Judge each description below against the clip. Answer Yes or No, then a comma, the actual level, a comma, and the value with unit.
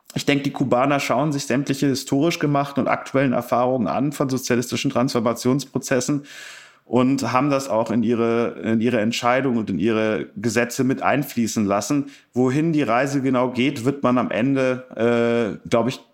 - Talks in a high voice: No, low, 130 Hz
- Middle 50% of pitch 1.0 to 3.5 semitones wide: Yes, average, 2.8 semitones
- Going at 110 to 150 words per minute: No, average, 165 wpm